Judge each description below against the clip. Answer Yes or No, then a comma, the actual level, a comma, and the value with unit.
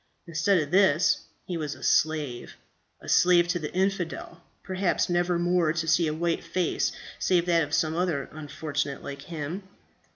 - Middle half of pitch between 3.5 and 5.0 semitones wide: No, narrow, 2.5 semitones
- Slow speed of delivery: No, average, 165 wpm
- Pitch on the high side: No, medium, 170 Hz